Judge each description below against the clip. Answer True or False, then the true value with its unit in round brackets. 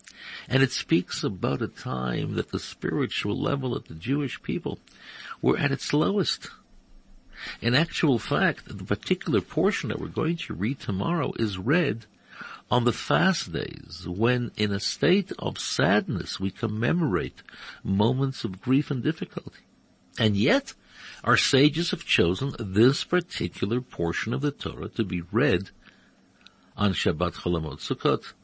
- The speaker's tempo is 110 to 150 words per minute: True (140 wpm)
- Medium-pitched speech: False (120 Hz)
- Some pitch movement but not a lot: False (6.7 semitones)